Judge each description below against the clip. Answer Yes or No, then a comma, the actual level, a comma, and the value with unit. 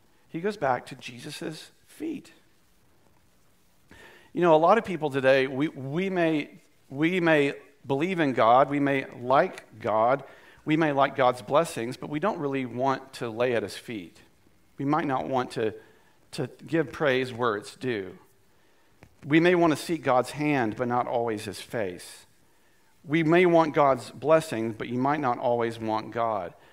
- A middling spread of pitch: Yes, average, 4.7 semitones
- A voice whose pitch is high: No, medium, 140 Hz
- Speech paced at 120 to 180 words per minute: Yes, average, 170 wpm